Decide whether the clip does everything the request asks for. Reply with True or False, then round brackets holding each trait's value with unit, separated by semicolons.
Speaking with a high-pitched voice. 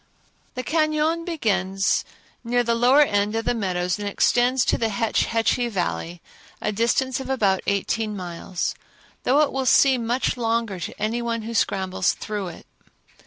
True (230 Hz)